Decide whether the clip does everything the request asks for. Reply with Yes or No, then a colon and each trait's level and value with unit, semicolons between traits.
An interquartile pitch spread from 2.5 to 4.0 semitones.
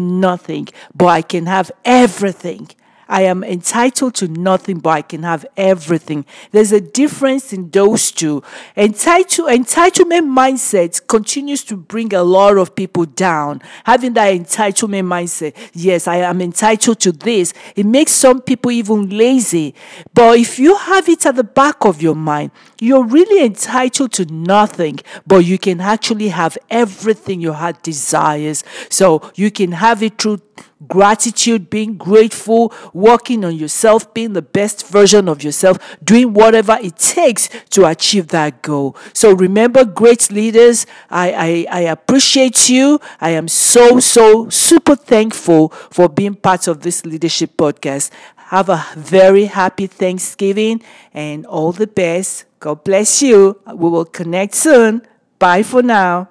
No: average, 5.0 semitones